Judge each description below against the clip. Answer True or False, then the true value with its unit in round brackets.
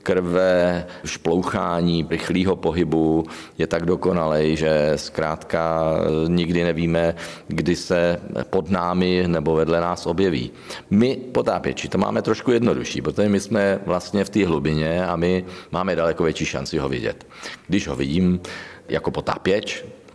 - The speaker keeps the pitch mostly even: True (2.2 semitones)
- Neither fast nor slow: True (135 wpm)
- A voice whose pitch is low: True (85 Hz)